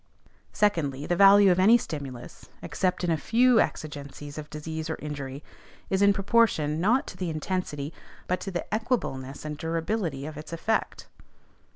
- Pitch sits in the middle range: Yes, medium, 165 Hz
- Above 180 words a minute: No, average, 160 wpm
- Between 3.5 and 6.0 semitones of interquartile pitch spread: Yes, average, 5.1 semitones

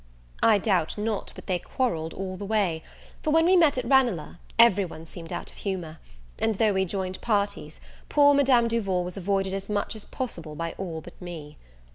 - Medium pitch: No, high, 195 Hz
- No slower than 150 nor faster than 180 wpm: No, average, 195 wpm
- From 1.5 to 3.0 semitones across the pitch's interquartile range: No, average, 4.8 semitones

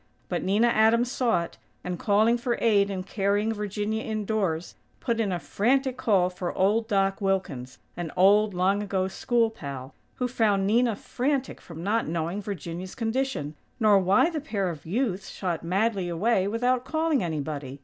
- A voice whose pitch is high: Yes, high, 205 Hz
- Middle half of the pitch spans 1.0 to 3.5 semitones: No, average, 4.1 semitones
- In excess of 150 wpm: Yes, average, 165 wpm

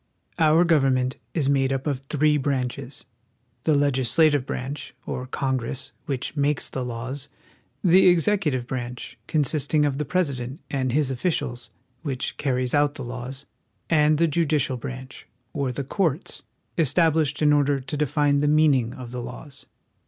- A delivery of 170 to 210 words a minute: No, average, 160 wpm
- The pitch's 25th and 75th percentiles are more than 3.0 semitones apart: No, average, 2.7 semitones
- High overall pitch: No, medium, 140 Hz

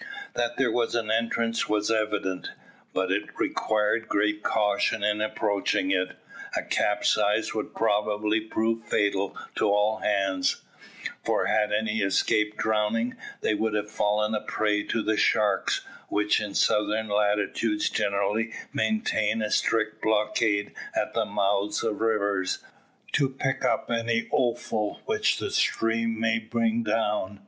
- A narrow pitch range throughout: Yes, narrow, 1.5 semitones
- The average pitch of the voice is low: Yes, low, 105 Hz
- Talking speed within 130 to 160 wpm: Yes, average, 140 wpm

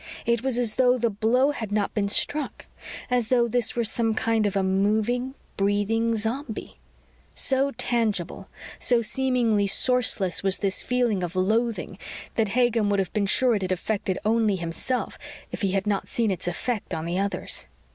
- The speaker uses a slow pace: No, average, 175 wpm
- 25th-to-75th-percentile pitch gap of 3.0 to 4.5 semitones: Yes, average, 3.5 semitones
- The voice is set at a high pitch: Yes, high, 220 Hz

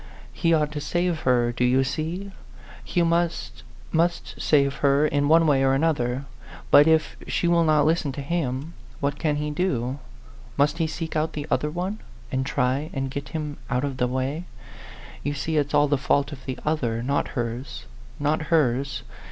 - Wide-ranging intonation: No, average, 3.1 semitones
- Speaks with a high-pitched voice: No, medium, 145 Hz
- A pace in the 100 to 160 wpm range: No, average, 185 wpm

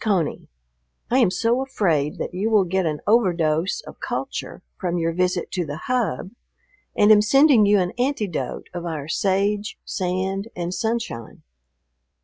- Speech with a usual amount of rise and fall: Yes, average, 4.1 semitones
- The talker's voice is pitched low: No, high, 190 Hz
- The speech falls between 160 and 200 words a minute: No, average, 150 wpm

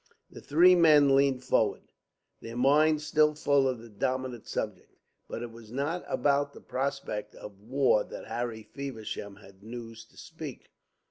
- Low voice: Yes, low, 130 Hz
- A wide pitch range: No, average, 3.9 semitones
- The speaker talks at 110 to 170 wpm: Yes, average, 155 wpm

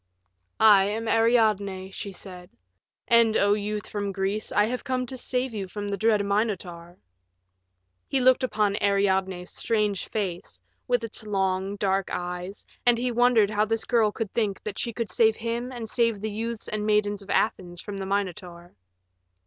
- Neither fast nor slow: Yes, average, 170 wpm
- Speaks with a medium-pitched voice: No, high, 210 Hz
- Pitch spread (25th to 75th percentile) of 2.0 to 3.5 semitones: Yes, average, 2.7 semitones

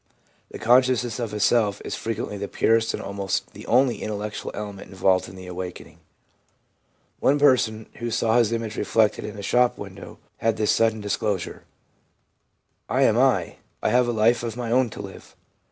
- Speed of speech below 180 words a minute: No, average, 185 wpm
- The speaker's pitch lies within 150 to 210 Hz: No, low, 110 Hz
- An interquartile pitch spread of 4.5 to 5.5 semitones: No, average, 2.8 semitones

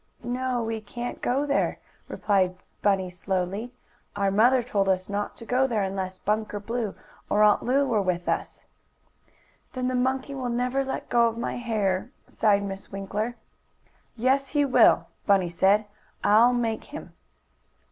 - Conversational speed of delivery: Yes, average, 155 wpm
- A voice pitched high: Yes, high, 220 Hz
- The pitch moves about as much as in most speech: Yes, average, 4.0 semitones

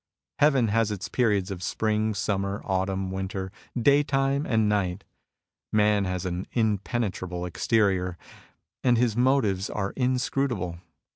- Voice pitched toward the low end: Yes, low, 105 Hz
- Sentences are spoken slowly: Yes, slow, 120 wpm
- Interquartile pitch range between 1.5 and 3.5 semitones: No, average, 4.0 semitones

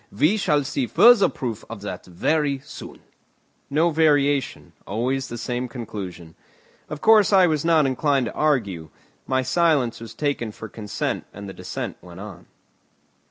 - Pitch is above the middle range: No, low, 130 Hz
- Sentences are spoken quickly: No, average, 155 wpm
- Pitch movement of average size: No, wide, 6.2 semitones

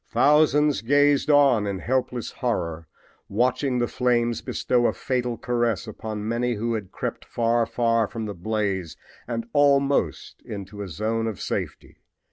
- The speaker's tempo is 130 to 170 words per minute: Yes, average, 145 wpm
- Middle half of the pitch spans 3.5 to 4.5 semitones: No, average, 3.0 semitones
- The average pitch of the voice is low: Yes, low, 115 Hz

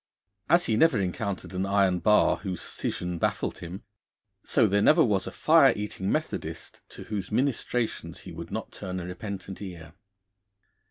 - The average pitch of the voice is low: Yes, low, 100 Hz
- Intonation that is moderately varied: Yes, average, 3.3 semitones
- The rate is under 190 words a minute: Yes, average, 160 wpm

